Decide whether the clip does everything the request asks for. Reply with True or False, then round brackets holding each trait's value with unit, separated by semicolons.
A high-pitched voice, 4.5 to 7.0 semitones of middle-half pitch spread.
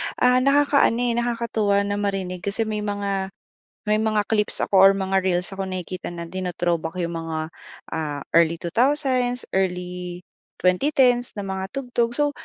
True (195 Hz; 4.8 semitones)